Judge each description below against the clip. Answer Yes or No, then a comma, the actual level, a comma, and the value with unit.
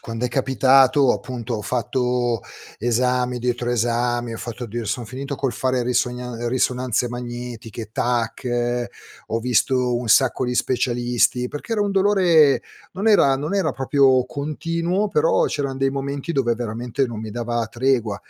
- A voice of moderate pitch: No, low, 125 Hz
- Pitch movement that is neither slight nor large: No, narrow, 2.2 semitones